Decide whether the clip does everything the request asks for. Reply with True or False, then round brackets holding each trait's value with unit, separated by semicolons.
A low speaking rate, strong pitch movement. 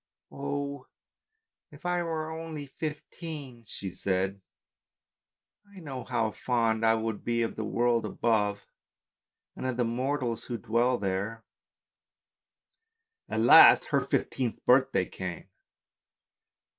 False (115 wpm; 4.2 semitones)